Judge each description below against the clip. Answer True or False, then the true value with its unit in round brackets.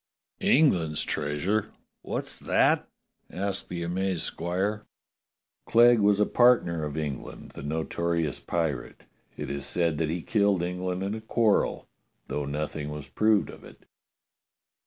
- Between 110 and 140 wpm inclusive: True (135 wpm)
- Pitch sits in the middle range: False (85 Hz)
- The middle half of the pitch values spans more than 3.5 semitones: True (4.9 semitones)